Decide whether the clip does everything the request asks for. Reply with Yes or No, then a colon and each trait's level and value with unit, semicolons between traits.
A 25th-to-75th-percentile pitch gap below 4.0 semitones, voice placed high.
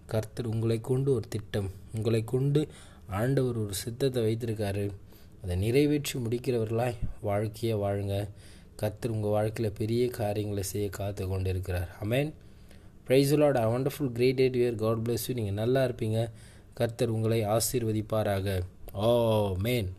No: average, 3.3 semitones; low, 110 Hz